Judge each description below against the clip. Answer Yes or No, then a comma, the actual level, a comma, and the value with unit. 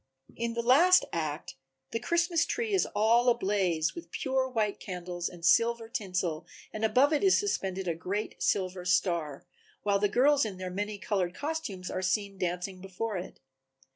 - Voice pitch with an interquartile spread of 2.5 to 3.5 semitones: No, average, 4.9 semitones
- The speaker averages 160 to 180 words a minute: Yes, average, 170 wpm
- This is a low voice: No, high, 205 Hz